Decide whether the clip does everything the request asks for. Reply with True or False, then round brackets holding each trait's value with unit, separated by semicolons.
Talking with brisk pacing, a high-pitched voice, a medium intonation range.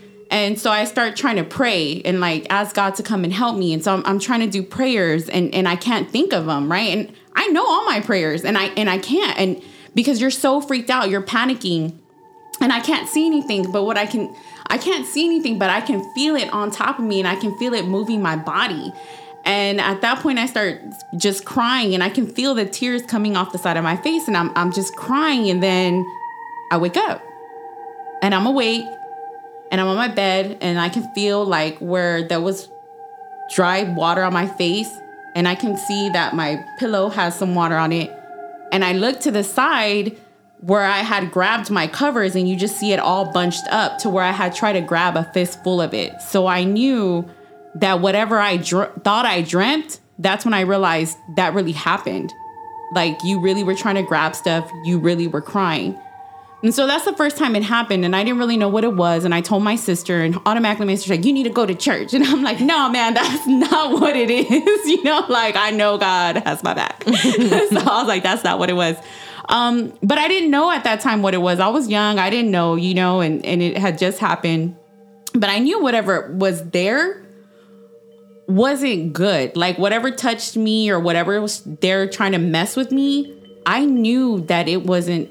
False (225 wpm; 205 Hz; 5.7 semitones)